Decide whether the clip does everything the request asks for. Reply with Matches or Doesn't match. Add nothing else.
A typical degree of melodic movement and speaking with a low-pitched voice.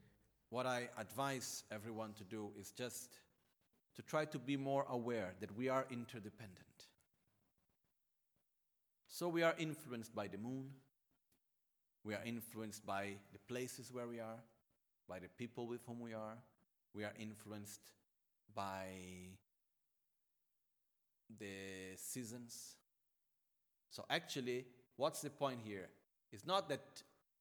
Matches